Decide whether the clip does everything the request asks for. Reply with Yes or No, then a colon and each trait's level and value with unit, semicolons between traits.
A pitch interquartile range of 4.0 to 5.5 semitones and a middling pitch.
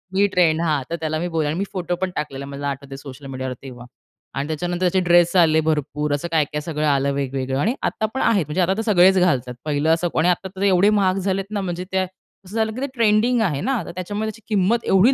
Yes: average, 4.8 semitones; medium, 175 Hz